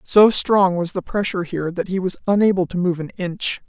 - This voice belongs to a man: No, female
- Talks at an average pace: No, fast, 230 wpm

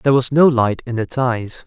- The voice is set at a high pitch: No, low, 125 Hz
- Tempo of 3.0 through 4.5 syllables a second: No, 5.0 syllables/s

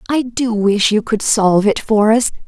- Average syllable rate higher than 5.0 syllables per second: No, 4.7 syllables/s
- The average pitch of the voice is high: Yes, high, 220 Hz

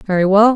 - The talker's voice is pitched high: Yes, high, 205 Hz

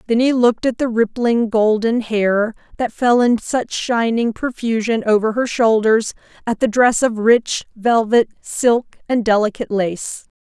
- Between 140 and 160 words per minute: Yes, average, 155 wpm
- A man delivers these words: No, female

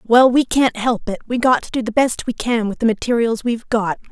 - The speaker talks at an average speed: No, fast, 260 wpm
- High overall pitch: Yes, high, 235 Hz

